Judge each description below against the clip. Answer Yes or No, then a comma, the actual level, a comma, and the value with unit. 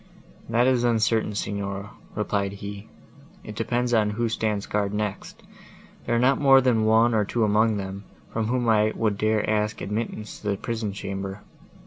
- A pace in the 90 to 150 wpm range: No, average, 175 wpm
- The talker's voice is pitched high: No, low, 110 Hz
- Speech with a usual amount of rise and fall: No, narrow, 2.2 semitones